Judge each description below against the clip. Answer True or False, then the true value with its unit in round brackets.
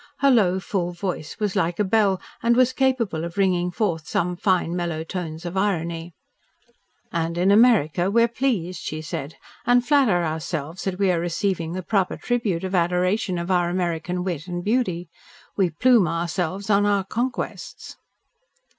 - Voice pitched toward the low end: False (180 Hz)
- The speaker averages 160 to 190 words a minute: True (165 wpm)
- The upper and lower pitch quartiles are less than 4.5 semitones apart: True (3.2 semitones)